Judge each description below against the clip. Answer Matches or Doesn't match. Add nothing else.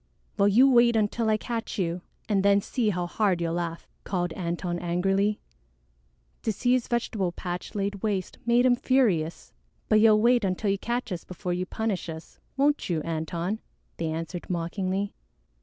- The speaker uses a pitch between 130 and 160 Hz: Doesn't match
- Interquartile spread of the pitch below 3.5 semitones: Doesn't match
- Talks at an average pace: Matches